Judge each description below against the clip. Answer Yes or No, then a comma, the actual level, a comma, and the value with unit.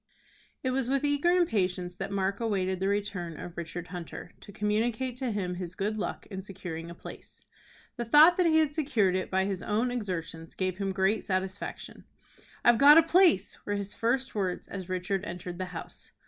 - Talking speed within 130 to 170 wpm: No, average, 190 wpm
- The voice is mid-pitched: No, high, 200 Hz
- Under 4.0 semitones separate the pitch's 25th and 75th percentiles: No, average, 4.7 semitones